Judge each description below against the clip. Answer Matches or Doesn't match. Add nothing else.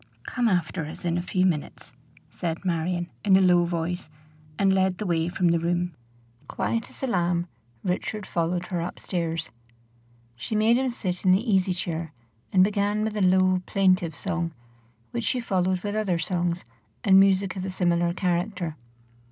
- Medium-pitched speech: Matches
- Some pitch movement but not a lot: Doesn't match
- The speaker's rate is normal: Matches